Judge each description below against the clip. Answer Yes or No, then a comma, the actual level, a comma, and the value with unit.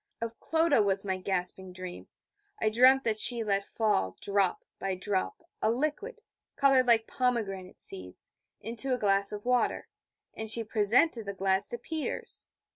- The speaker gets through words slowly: No, average, 155 wpm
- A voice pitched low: No, high, 215 Hz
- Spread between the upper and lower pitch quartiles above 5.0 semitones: No, average, 4.3 semitones